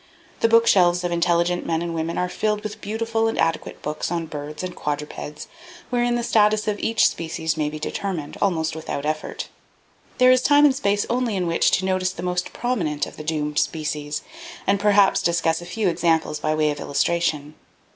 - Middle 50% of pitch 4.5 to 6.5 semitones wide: Yes, average, 5.0 semitones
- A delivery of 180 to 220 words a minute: Yes, average, 190 wpm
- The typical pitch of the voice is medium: Yes, medium, 175 Hz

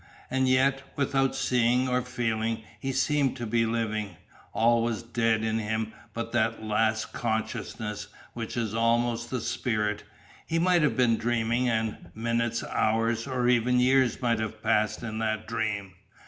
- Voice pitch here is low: Yes, low, 115 Hz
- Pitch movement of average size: No, narrow, 2.1 semitones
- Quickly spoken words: No, average, 155 wpm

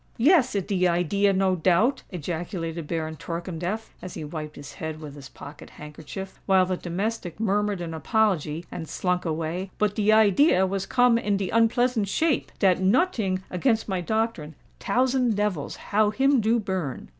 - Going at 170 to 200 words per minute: No, average, 155 wpm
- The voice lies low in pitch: No, high, 190 Hz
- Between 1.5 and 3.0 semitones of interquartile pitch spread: No, average, 4.7 semitones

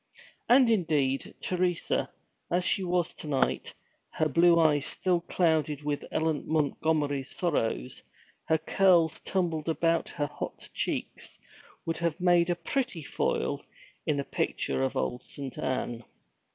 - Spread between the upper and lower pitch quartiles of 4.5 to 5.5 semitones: No, average, 3.2 semitones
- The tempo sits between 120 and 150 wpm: Yes, slow, 135 wpm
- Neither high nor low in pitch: Yes, medium, 160 Hz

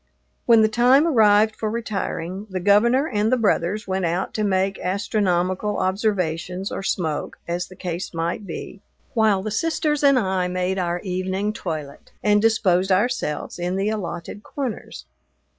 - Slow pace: No, average, 155 wpm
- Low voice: No, high, 195 Hz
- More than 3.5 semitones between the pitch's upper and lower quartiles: No, average, 3.1 semitones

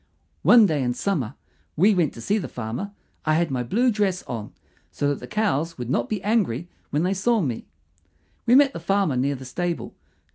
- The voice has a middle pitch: Yes, medium, 170 Hz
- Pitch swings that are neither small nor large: No, wide, 7.6 semitones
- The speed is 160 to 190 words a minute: No, fast, 205 wpm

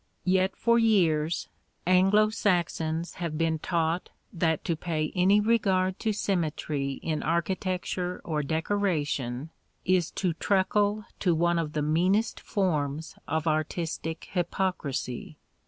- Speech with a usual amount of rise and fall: Yes, average, 3.2 semitones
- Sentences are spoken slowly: Yes, slow, 120 wpm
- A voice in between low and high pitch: Yes, medium, 170 Hz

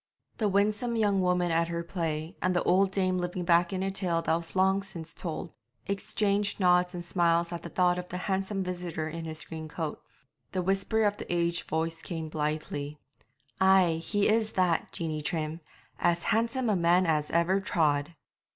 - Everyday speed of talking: Yes, average, 185 wpm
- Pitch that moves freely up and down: No, average, 2.7 semitones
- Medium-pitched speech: Yes, medium, 175 Hz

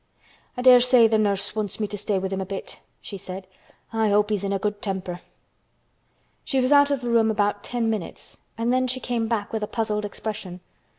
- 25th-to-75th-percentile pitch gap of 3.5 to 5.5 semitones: No, average, 2.9 semitones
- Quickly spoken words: Yes, fast, 220 wpm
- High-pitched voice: Yes, high, 215 Hz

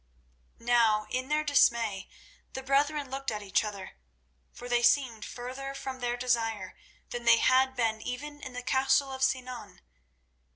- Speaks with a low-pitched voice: No, very high, 250 Hz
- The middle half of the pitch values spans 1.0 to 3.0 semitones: Yes, narrow, 2.4 semitones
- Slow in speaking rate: No, average, 155 wpm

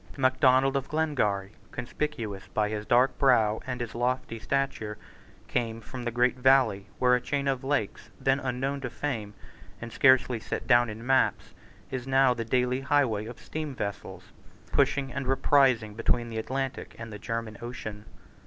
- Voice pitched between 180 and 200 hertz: No, low, 125 Hz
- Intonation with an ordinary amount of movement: Yes, average, 3.2 semitones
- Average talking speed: Yes, average, 160 wpm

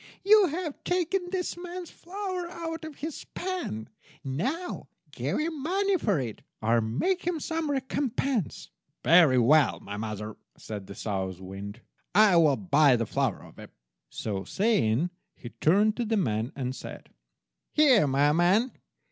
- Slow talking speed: No, average, 150 wpm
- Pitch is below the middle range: No, high, 200 Hz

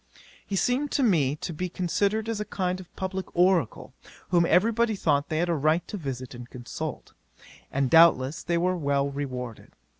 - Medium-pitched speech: Yes, medium, 170 Hz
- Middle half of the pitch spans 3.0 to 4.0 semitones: No, average, 5.1 semitones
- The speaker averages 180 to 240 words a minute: Yes, average, 185 wpm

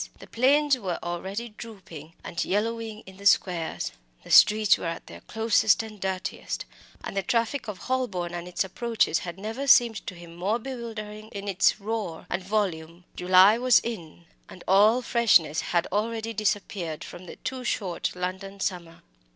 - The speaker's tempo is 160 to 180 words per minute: Yes, average, 165 wpm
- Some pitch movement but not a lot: Yes, average, 4.1 semitones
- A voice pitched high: Yes, high, 200 Hz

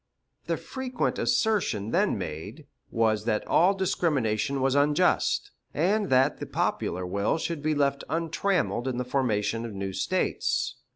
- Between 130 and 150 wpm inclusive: Yes, average, 140 wpm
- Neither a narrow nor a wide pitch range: No, wide, 7.6 semitones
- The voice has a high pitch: No, low, 135 Hz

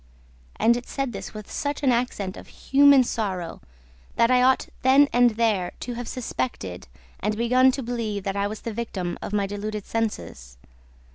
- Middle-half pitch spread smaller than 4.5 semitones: Yes, average, 3.9 semitones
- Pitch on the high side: Yes, high, 225 Hz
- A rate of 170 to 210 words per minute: Yes, average, 180 wpm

